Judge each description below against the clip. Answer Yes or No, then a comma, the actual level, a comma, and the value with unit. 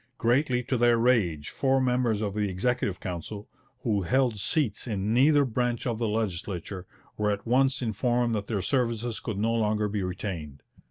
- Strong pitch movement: No, average, 3.5 semitones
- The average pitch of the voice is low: Yes, low, 110 Hz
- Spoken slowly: No, average, 170 wpm